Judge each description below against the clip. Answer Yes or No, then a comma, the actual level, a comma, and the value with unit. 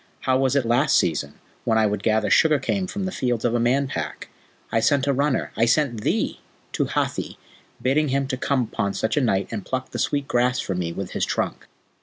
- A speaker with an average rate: No, fast, 225 wpm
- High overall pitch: No, low, 125 Hz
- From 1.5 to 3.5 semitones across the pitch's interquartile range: No, average, 4.0 semitones